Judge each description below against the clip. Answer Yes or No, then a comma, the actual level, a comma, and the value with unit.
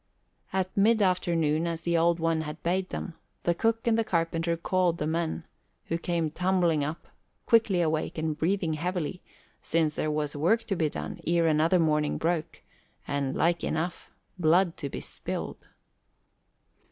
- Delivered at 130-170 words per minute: Yes, average, 160 wpm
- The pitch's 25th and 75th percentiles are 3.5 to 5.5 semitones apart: No, narrow, 2.4 semitones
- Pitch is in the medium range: Yes, medium, 170 Hz